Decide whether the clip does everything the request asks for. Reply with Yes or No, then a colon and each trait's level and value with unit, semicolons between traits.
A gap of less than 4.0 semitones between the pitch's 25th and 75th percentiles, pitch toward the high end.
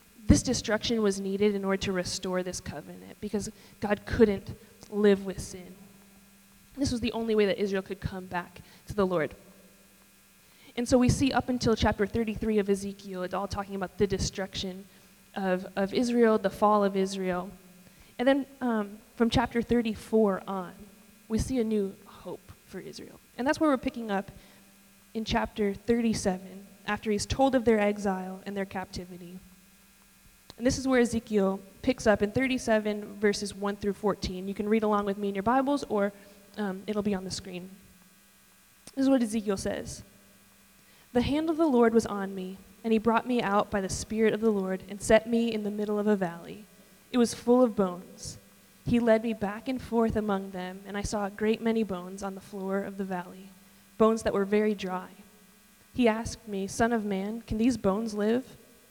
Yes: narrow, 2.5 semitones; high, 205 Hz